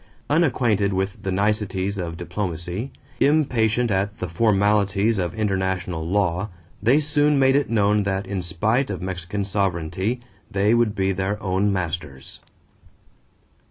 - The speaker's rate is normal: No, slow, 130 wpm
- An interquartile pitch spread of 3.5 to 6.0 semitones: No, average, 2.9 semitones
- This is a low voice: Yes, low, 100 Hz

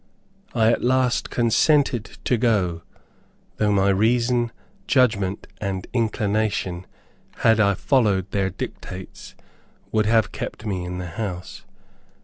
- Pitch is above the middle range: No, low, 105 Hz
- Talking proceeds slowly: Yes, slow, 120 wpm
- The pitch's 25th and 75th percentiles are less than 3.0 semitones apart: No, average, 3.7 semitones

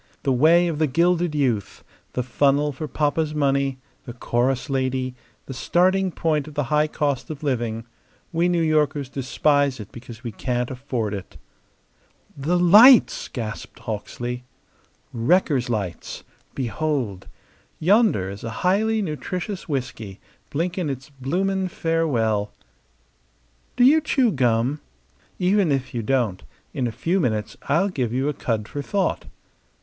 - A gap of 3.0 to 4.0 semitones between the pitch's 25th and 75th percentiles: No, wide, 5.5 semitones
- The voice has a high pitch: No, medium, 140 Hz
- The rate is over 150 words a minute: No, average, 140 wpm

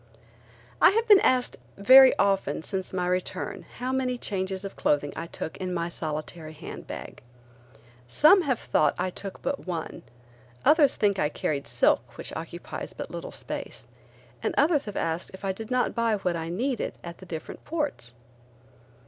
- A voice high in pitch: Yes, high, 195 Hz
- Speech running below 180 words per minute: Yes, average, 170 wpm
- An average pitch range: No, wide, 7.2 semitones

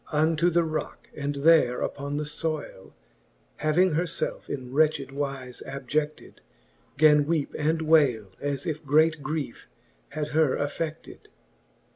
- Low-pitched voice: No, medium, 150 Hz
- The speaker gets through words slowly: Yes, slow, 130 wpm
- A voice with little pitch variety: Yes, narrow, 2.0 semitones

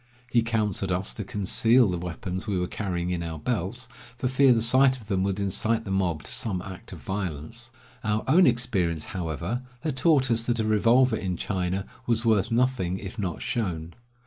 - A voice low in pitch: Yes, low, 105 Hz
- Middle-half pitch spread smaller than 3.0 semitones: No, average, 4.6 semitones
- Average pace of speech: Yes, average, 195 wpm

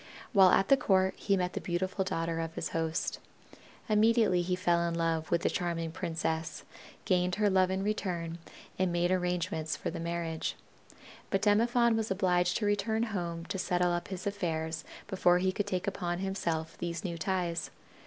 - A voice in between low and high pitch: Yes, medium, 180 Hz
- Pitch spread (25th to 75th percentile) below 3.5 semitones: Yes, narrow, 2.4 semitones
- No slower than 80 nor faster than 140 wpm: No, average, 175 wpm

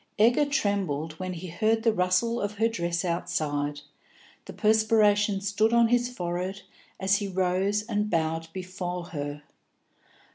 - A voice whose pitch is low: No, high, 195 Hz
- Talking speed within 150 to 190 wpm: No, average, 140 wpm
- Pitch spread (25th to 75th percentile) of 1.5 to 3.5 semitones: No, average, 4.0 semitones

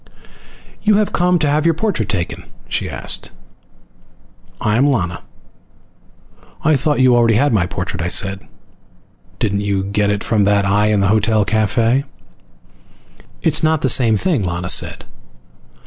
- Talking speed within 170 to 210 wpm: No, average, 150 wpm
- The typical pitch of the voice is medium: No, low, 110 Hz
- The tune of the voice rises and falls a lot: Yes, wide, 5.8 semitones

